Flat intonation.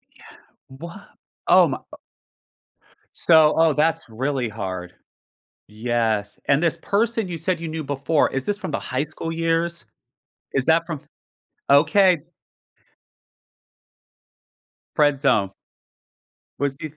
No: average, 3.9 semitones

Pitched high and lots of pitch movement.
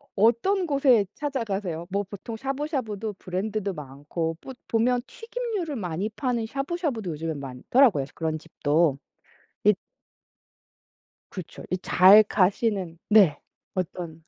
Yes: high, 205 Hz; wide, 6.9 semitones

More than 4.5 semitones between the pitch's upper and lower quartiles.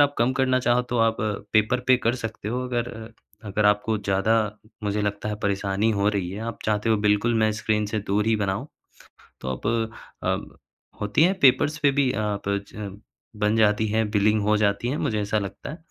No: narrow, 2.5 semitones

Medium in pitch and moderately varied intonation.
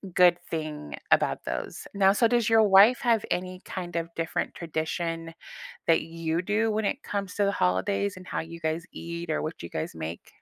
Yes: medium, 175 Hz; average, 3.7 semitones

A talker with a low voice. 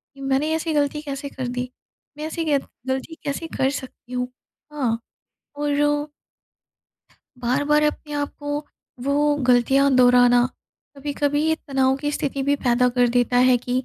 No: very high, 275 Hz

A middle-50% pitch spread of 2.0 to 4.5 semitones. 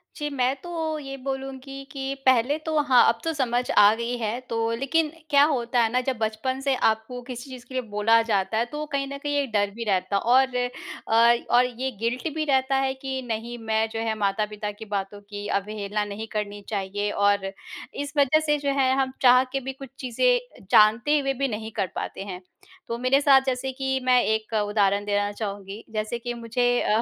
Yes: average, 3.9 semitones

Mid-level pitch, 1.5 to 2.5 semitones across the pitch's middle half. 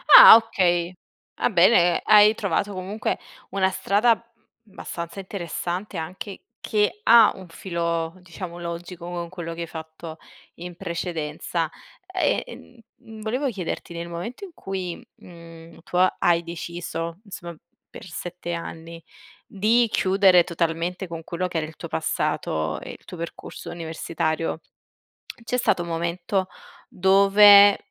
No: medium, 175 Hz; average, 2.9 semitones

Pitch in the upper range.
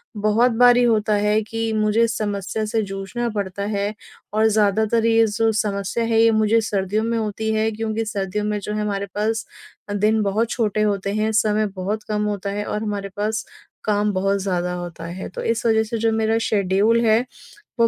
Yes: high, 215 Hz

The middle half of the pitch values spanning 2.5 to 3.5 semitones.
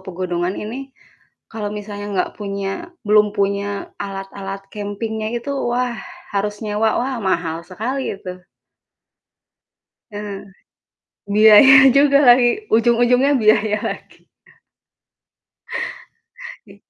Yes: average, 3.2 semitones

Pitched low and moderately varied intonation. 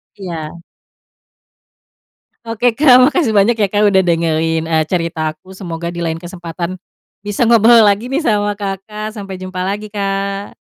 No: high, 195 Hz; average, 3.8 semitones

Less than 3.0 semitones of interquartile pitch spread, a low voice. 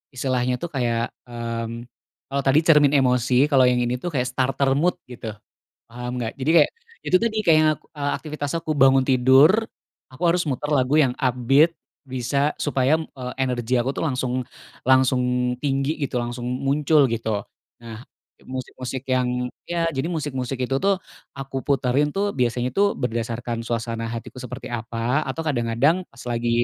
Yes: narrow, 2.6 semitones; low, 130 Hz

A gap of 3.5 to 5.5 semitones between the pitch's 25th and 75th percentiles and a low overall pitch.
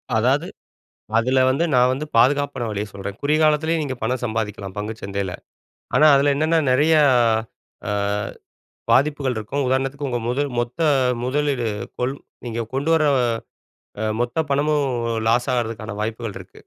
Yes: average, 4.2 semitones; low, 130 Hz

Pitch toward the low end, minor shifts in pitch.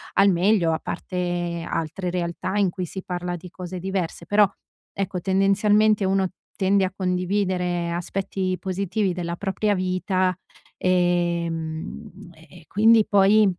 No: medium, 185 Hz; narrow, 1.9 semitones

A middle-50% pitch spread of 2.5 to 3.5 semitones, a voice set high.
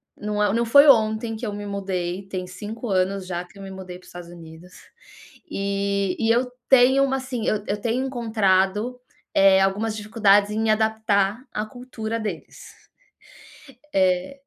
Yes: average, 2.9 semitones; high, 210 Hz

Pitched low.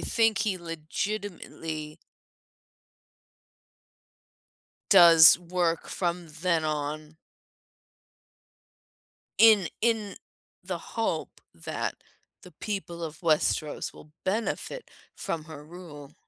No: medium, 170 Hz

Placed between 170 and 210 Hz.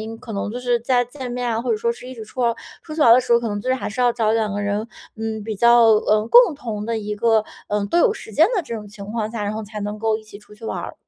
No: high, 225 Hz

